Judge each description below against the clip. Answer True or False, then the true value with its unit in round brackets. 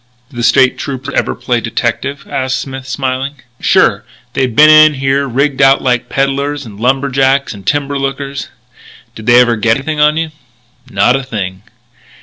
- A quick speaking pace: False (170 wpm)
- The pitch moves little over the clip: True (2.2 semitones)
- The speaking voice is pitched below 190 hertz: True (135 Hz)